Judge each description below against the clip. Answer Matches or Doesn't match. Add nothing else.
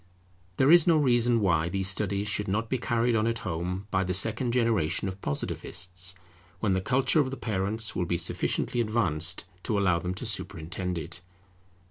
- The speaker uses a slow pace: Doesn't match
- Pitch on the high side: Doesn't match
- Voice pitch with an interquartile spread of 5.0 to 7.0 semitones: Doesn't match